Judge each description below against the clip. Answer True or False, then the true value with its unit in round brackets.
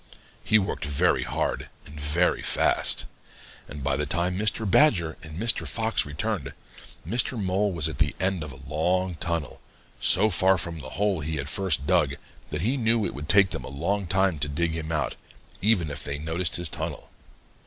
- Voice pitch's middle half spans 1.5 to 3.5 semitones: False (4.5 semitones)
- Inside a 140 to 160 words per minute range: False (190 wpm)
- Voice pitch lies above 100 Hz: False (85 Hz)